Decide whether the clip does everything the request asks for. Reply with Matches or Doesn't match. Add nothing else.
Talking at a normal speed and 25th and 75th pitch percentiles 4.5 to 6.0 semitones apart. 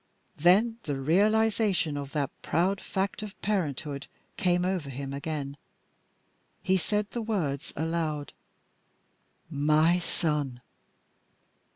Doesn't match